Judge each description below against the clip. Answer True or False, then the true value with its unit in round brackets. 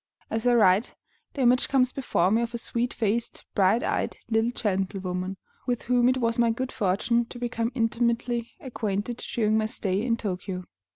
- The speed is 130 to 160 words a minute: False (175 wpm)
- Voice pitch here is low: False (230 Hz)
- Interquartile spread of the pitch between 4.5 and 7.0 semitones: False (3.0 semitones)